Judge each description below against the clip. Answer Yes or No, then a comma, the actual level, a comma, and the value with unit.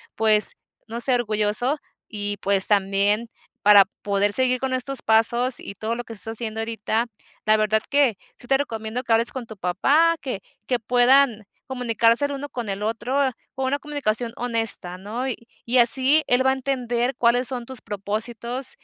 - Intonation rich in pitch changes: No, average, 3.3 semitones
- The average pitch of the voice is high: Yes, high, 235 Hz